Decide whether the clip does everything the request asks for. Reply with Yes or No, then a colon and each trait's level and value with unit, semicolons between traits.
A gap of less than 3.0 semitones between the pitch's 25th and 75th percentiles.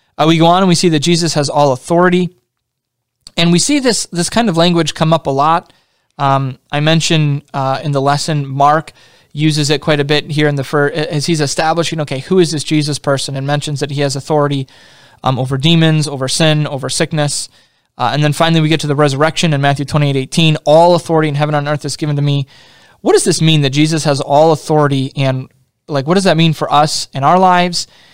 Yes: narrow, 2.5 semitones